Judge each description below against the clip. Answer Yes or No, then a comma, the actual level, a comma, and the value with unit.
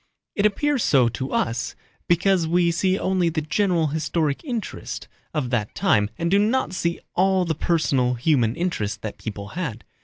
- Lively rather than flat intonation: Yes, wide, 6.9 semitones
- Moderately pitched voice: Yes, medium, 165 Hz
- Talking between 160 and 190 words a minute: Yes, average, 165 wpm